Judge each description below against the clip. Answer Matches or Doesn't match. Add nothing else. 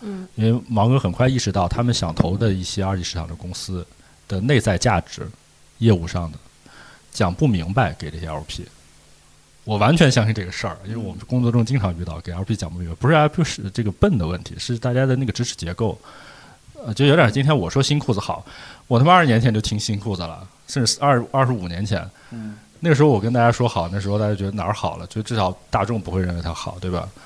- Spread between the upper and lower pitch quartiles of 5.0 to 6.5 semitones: Matches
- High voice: Doesn't match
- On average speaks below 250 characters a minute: Doesn't match